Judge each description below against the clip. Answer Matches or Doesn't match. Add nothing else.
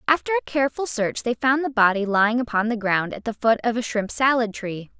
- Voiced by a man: Doesn't match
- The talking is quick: Matches